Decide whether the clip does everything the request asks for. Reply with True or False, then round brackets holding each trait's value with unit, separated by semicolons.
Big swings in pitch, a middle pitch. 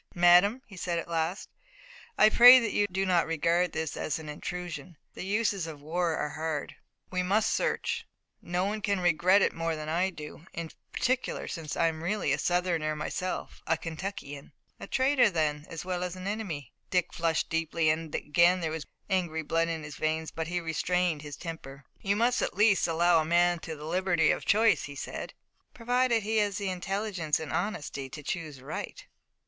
False (3.4 semitones; 175 Hz)